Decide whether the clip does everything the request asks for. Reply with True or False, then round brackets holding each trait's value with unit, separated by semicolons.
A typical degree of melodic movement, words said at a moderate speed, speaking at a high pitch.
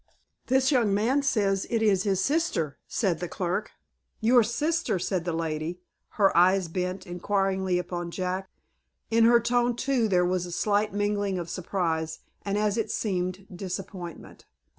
True (3.6 semitones; 155 wpm; 195 Hz)